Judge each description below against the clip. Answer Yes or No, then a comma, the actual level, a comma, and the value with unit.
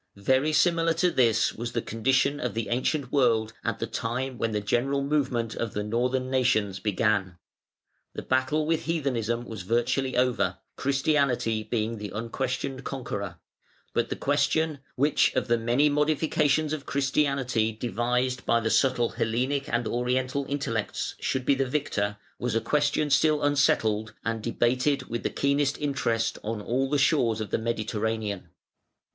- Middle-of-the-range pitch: No, low, 125 Hz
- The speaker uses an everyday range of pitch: Yes, average, 3.7 semitones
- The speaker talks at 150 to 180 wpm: Yes, average, 155 wpm